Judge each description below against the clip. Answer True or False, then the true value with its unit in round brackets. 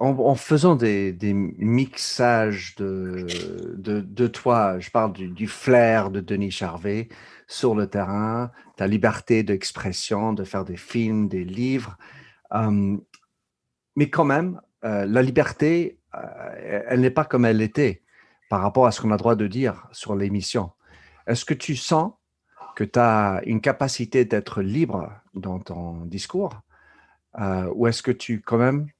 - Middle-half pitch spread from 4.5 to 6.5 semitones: False (4.1 semitones)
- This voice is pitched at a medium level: False (110 Hz)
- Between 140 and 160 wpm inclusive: True (155 wpm)